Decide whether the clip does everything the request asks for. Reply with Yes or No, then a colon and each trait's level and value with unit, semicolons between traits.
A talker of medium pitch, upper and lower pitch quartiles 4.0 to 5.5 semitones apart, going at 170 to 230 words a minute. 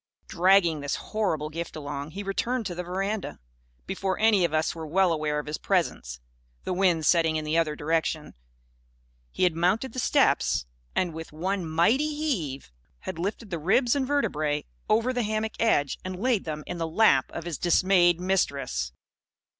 Yes: medium, 175 Hz; average, 4.6 semitones; average, 175 wpm